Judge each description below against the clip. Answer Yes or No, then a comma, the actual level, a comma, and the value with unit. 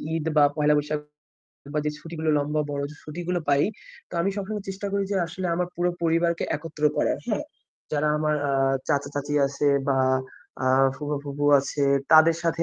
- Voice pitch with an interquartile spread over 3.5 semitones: No, narrow, 2.6 semitones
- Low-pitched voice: No, medium, 155 Hz